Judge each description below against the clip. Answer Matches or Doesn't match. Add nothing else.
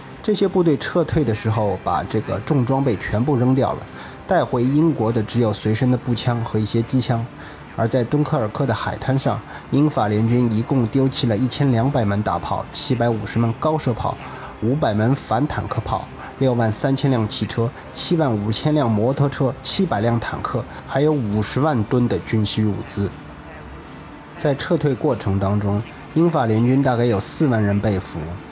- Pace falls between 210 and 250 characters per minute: Doesn't match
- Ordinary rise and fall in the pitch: Matches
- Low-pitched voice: Matches